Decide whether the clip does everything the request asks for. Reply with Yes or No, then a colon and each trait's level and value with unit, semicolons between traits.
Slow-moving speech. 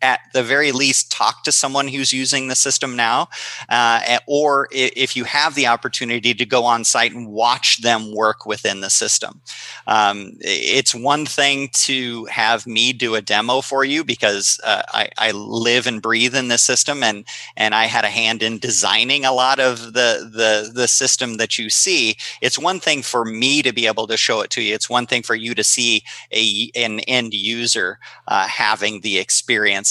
No: average, 195 wpm